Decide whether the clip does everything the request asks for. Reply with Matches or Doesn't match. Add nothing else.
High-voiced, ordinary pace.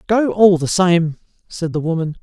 Doesn't match